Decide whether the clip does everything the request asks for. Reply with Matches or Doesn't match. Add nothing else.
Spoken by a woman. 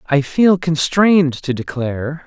Doesn't match